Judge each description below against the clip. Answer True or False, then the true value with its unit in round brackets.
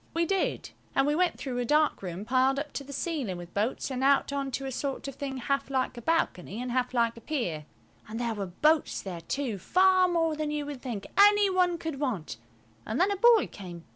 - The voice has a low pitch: False (270 Hz)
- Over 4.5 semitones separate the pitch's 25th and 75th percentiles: True (5.2 semitones)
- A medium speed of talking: False (230 wpm)